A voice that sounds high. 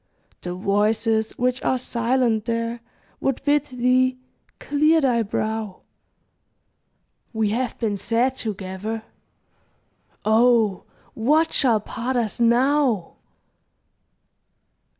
Yes: high, 235 Hz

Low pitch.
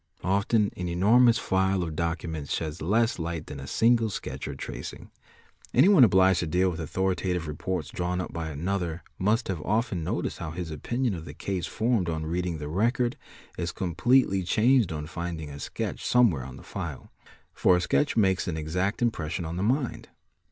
Yes: very low, 90 Hz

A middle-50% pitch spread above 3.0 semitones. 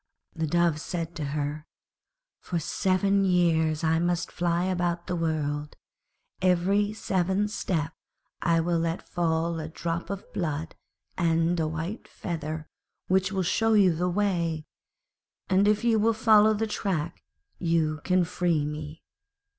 No: average, 2.7 semitones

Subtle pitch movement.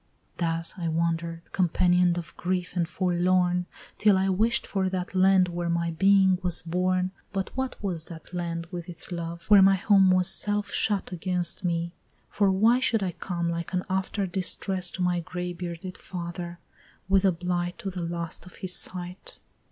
Yes: narrow, 1.8 semitones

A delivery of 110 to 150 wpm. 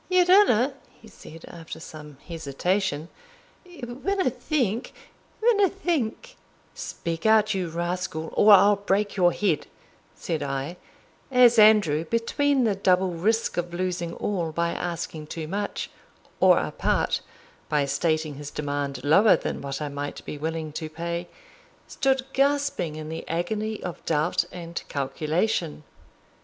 Yes: slow, 135 wpm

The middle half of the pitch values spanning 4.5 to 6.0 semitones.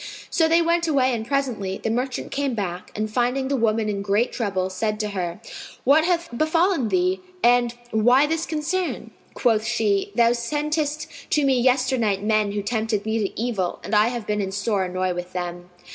Yes: average, 5.2 semitones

